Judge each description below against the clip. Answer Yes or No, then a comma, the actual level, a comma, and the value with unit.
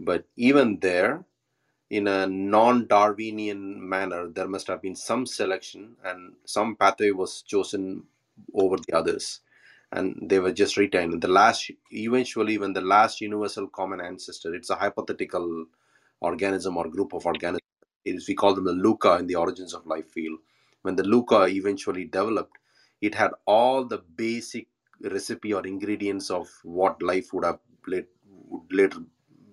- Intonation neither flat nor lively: No, narrow, 2.0 semitones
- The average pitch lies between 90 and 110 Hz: Yes, very low, 95 Hz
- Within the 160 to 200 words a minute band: No, average, 150 wpm